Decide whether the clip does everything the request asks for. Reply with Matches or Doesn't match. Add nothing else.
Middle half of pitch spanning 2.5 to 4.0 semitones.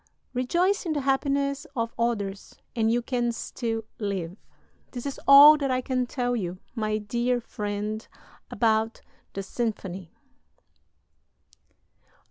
Matches